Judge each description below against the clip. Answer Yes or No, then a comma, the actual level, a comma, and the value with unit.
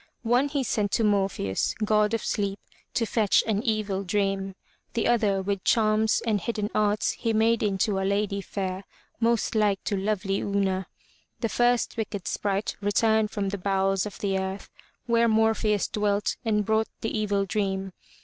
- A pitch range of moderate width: No, narrow, 2.0 semitones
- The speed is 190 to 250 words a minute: No, average, 165 wpm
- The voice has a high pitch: Yes, high, 205 Hz